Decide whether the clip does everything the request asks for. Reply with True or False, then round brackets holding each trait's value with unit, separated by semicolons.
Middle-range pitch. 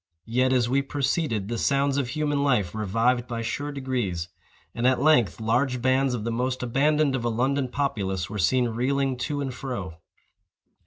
False (125 Hz)